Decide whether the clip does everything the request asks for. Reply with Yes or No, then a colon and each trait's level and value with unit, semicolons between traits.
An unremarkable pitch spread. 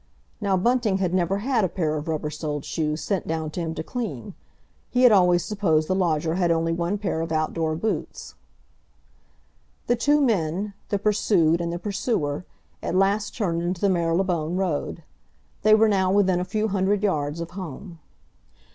Yes: average, 3.9 semitones